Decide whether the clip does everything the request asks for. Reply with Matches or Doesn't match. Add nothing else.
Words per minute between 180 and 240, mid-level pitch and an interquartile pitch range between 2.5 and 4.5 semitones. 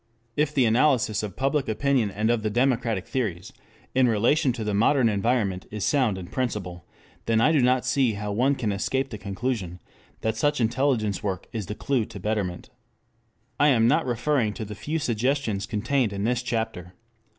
Doesn't match